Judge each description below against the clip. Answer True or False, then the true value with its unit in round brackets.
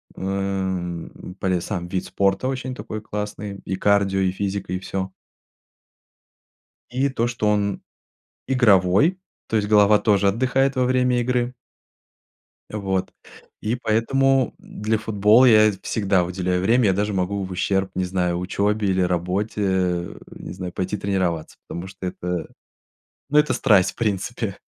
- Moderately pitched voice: False (100 Hz)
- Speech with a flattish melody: False (3.1 semitones)